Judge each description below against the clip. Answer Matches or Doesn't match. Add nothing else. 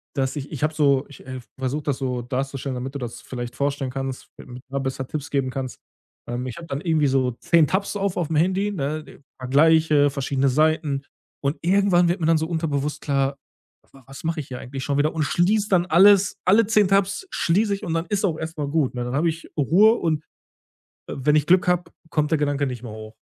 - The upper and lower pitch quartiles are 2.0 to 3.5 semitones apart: Doesn't match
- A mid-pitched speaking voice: Matches